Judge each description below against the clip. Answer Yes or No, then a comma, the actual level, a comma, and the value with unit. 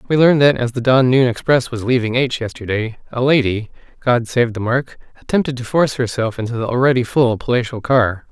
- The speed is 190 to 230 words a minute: Yes, average, 200 wpm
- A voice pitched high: No, low, 125 Hz